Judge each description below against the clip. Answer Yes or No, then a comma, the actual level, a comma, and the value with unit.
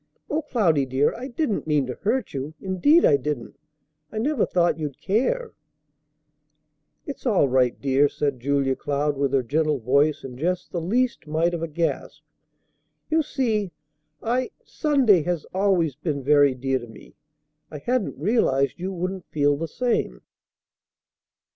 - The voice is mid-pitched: Yes, medium, 160 Hz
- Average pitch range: No, wide, 7.4 semitones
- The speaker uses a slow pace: No, average, 155 wpm